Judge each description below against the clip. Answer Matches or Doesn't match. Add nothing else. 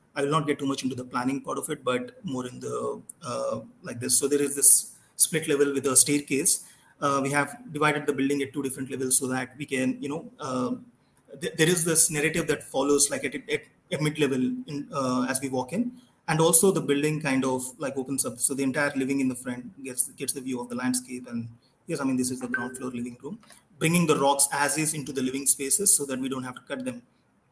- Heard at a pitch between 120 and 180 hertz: Matches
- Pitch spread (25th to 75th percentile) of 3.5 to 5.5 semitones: Doesn't match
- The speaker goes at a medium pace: Doesn't match